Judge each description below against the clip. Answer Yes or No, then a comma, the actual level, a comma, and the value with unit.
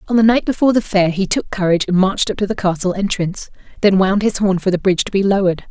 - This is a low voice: No, high, 195 Hz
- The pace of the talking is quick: Yes, fast, 275 wpm